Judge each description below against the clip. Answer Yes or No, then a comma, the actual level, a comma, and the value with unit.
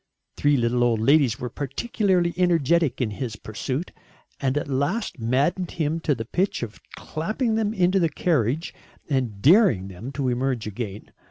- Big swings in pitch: Yes, wide, 6.4 semitones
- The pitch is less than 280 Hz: Yes, medium, 140 Hz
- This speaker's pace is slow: No, average, 160 wpm